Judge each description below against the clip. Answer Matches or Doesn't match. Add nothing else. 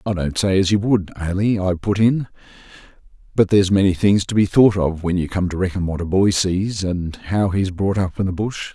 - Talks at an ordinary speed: Doesn't match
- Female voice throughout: Doesn't match